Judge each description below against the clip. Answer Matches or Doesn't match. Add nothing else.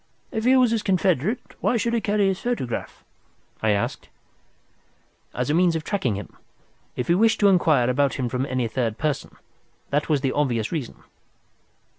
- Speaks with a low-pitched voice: Doesn't match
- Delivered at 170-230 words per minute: Matches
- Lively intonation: Matches